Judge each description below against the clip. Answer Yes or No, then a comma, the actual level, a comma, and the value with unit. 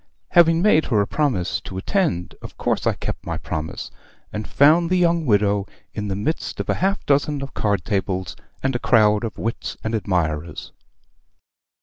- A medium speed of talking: Yes, average, 180 wpm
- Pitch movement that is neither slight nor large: No, wide, 7.8 semitones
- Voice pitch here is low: Yes, low, 110 Hz